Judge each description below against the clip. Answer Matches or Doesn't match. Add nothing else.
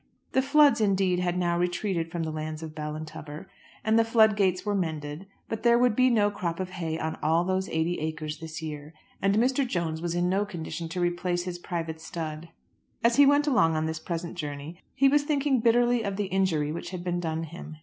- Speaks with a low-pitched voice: Doesn't match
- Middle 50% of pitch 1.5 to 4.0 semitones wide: Doesn't match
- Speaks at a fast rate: Matches